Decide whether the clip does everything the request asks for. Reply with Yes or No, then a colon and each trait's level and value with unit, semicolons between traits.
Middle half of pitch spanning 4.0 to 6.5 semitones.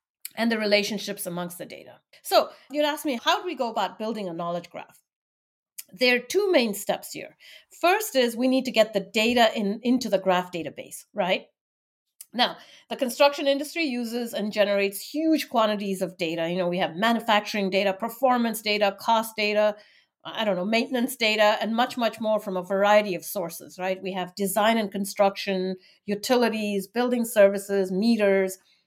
No: average, 3.6 semitones